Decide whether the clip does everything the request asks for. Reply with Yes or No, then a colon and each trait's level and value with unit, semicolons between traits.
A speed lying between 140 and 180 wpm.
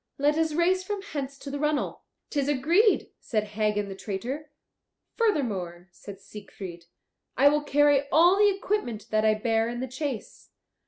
Yes: average, 160 wpm